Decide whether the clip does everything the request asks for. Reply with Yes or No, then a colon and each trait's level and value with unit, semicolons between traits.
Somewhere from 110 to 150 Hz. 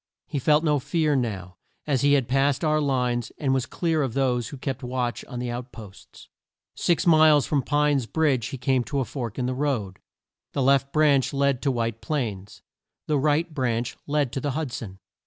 Yes: low, 135 Hz